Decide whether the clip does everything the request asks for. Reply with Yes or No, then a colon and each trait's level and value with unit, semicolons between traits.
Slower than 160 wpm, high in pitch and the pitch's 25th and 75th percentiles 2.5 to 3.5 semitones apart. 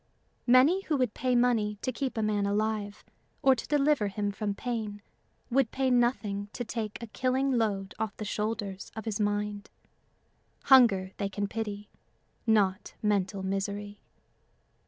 Yes: average, 150 wpm; high, 215 Hz; average, 3.2 semitones